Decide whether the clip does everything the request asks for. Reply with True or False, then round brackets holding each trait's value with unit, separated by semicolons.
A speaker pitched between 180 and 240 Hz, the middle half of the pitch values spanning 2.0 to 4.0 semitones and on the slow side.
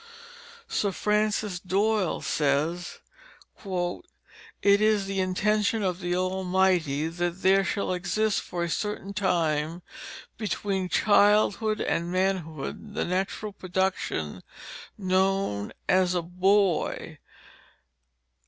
True (190 Hz; 2.5 semitones; 95 wpm)